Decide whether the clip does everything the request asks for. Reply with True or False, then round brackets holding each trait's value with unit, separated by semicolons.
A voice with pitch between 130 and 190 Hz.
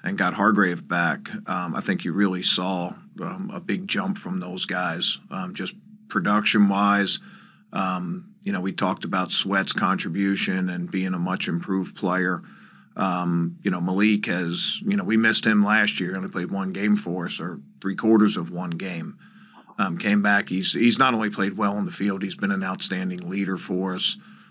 False (100 Hz)